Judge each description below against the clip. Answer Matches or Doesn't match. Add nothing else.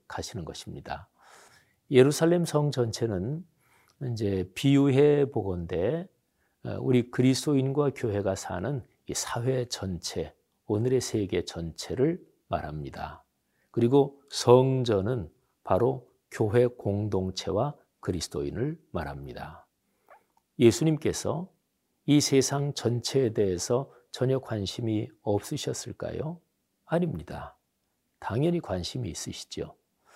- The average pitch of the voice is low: Matches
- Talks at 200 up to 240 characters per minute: Matches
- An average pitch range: Doesn't match